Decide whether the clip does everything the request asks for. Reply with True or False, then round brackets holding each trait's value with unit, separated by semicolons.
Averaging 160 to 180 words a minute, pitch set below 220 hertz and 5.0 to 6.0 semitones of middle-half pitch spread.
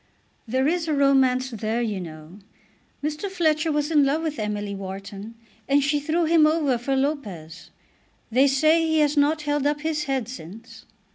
False (170 wpm; 275 Hz; 5.3 semitones)